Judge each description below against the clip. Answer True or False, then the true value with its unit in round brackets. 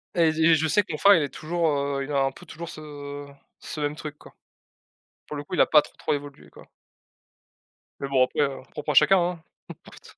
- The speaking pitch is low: False (150 Hz)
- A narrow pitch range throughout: True (2.2 semitones)